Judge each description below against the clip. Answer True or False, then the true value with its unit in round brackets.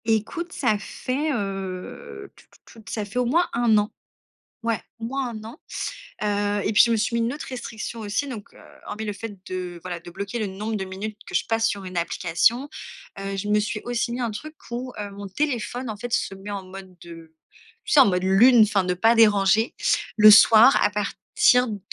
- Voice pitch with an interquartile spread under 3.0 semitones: False (3.3 semitones)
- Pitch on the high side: True (215 Hz)